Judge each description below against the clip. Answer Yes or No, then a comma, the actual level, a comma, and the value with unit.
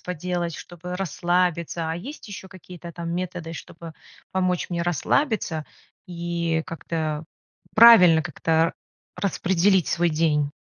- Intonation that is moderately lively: No, narrow, 1.8 semitones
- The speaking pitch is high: No, medium, 170 Hz